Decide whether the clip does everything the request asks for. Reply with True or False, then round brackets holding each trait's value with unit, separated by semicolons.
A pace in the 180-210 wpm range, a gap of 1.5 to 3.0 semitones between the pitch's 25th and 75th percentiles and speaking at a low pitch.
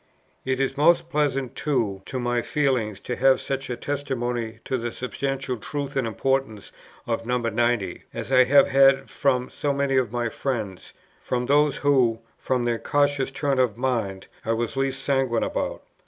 False (170 wpm; 2.6 semitones; 130 Hz)